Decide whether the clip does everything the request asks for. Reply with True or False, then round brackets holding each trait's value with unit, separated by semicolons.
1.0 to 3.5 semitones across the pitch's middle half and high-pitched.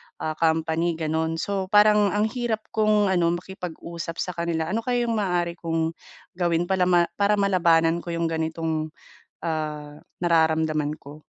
False (2.9 semitones; 170 Hz)